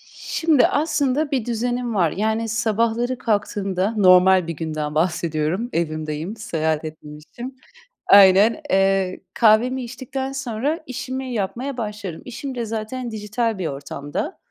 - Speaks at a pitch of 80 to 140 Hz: No, high, 215 Hz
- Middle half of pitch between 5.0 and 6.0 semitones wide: Yes, wide, 5.4 semitones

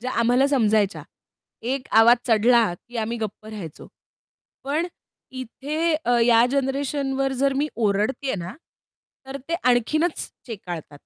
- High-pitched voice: Yes, high, 245 Hz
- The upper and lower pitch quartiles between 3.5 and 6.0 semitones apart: Yes, average, 3.8 semitones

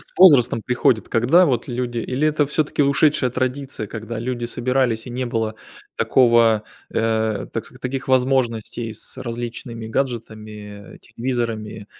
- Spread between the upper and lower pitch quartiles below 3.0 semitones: Yes, narrow, 2.6 semitones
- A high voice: No, low, 120 Hz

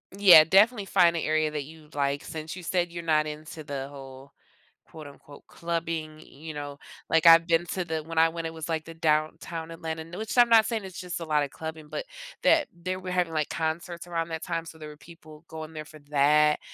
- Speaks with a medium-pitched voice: Yes, medium, 160 Hz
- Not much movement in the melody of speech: Yes, narrow, 1.9 semitones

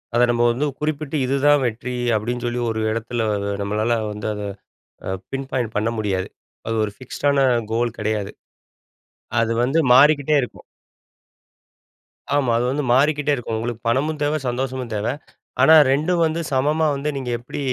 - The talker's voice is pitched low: Yes, low, 125 Hz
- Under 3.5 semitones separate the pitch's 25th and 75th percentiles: No, average, 4.1 semitones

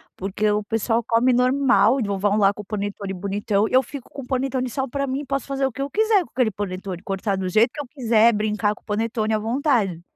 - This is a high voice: Yes, high, 225 Hz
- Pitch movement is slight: No, average, 4.4 semitones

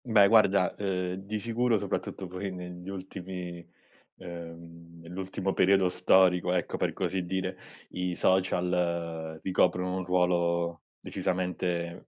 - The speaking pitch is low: Yes, very low, 90 Hz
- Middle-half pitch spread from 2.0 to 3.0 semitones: No, narrow, 1.6 semitones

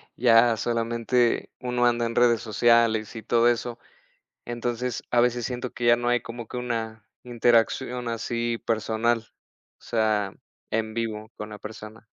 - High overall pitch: No, low, 115 Hz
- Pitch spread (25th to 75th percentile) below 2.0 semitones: Yes, narrow, 1.3 semitones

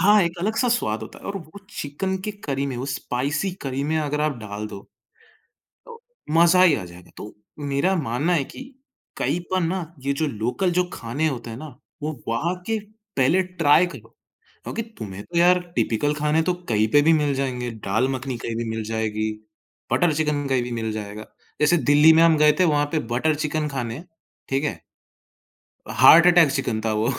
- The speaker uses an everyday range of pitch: No, wide, 6.0 semitones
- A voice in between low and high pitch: Yes, medium, 145 Hz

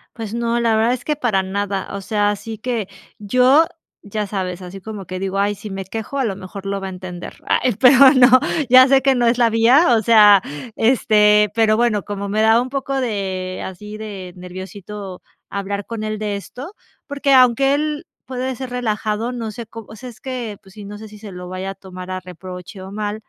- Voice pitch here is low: No, high, 215 Hz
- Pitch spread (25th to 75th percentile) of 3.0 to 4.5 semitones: Yes, average, 3.7 semitones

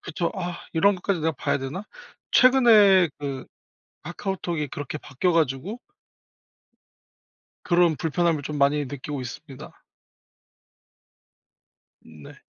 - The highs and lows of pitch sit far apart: No, average, 4.3 semitones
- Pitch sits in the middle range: Yes, medium, 160 Hz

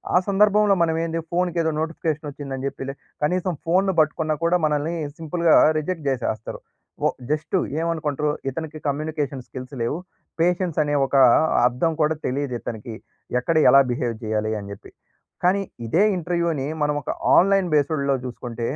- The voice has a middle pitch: Yes, medium, 155 Hz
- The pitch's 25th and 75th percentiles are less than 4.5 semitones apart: Yes, average, 3.9 semitones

